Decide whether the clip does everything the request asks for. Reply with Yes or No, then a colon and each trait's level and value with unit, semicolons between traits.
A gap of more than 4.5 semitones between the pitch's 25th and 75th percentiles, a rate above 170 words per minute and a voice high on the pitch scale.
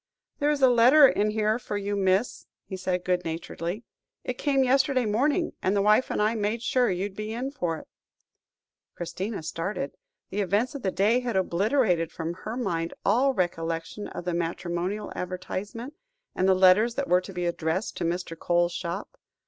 Yes: average, 5.1 semitones; average, 180 wpm; high, 200 Hz